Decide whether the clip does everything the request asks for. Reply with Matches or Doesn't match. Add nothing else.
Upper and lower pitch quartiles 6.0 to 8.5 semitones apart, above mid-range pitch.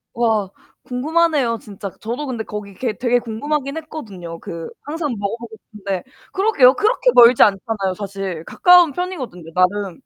Matches